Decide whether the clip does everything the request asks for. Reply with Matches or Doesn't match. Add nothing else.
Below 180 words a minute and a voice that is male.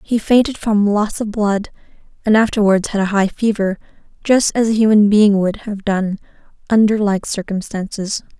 Doesn't match